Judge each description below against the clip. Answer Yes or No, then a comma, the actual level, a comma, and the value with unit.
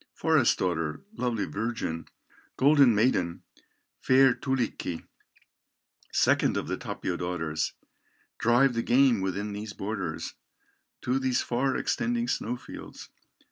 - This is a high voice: No, low, 115 Hz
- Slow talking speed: Yes, slow, 110 wpm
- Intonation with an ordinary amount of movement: No, wide, 5.7 semitones